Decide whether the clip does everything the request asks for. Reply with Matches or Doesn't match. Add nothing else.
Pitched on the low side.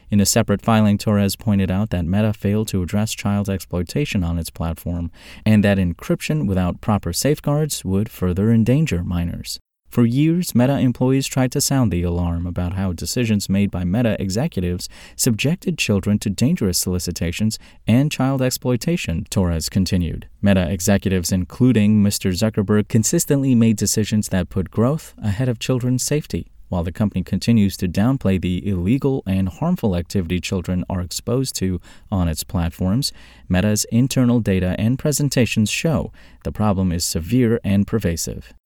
Matches